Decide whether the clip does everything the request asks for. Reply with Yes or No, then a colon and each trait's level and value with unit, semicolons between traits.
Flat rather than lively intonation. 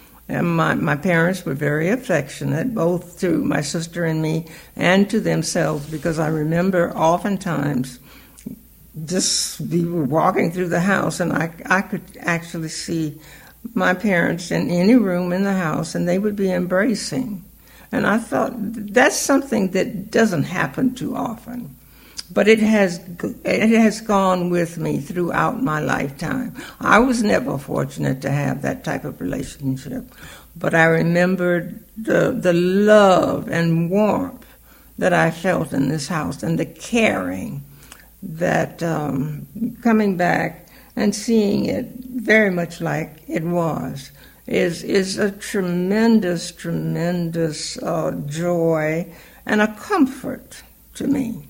No: average, 4.7 semitones